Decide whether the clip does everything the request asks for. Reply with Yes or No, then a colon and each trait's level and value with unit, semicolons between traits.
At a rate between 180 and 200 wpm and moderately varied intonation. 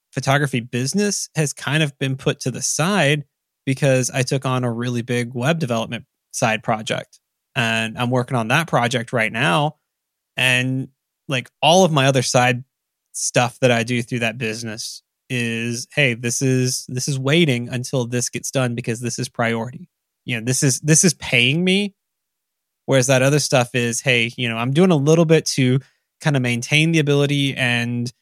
Yes: average, 185 wpm; average, 3.2 semitones